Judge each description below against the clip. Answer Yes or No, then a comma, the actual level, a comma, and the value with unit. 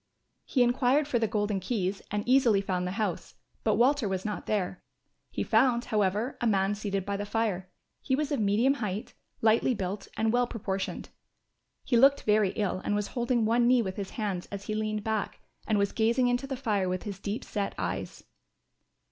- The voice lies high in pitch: Yes, high, 215 Hz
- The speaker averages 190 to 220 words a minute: Yes, average, 195 wpm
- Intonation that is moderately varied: Yes, average, 3.4 semitones